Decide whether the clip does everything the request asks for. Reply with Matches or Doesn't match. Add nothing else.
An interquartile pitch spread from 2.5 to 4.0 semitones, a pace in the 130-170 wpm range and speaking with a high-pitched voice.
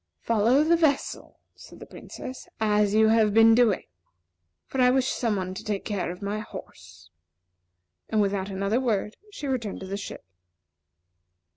Matches